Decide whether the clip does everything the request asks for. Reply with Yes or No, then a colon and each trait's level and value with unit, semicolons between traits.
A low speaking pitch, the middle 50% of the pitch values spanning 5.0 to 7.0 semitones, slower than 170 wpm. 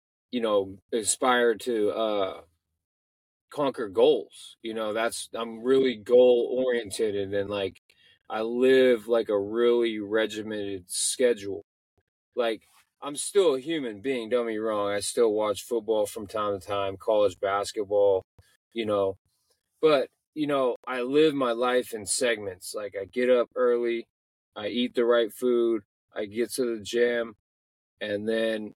No: low, 115 Hz; average, 3.6 semitones; average, 150 wpm